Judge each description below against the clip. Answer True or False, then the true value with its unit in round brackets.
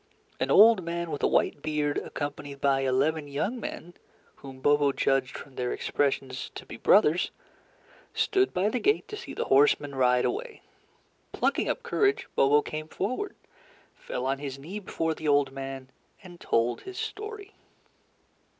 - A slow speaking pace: False (160 wpm)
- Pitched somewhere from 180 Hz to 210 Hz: False (145 Hz)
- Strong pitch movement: True (6.5 semitones)